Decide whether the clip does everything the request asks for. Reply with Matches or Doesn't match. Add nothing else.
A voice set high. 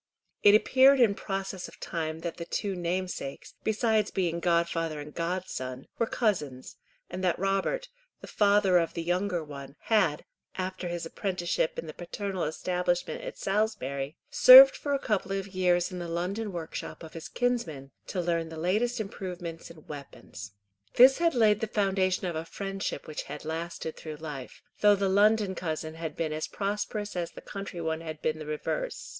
Doesn't match